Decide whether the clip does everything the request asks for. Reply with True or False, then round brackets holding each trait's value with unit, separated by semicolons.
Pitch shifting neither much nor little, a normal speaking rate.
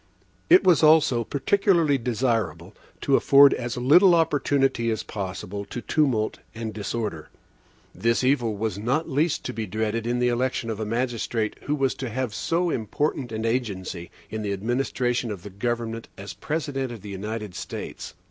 True (4.0 semitones; 165 wpm)